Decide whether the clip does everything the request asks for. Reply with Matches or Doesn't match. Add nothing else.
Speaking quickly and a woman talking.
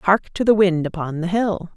Matches